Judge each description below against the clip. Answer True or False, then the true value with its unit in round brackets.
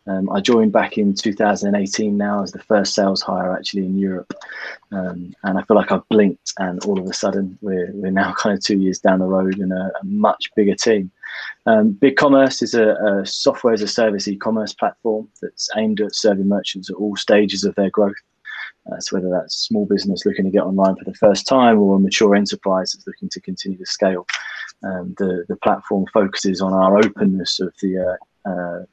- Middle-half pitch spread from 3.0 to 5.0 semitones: False (2.5 semitones)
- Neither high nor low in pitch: False (100 Hz)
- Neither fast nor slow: False (215 wpm)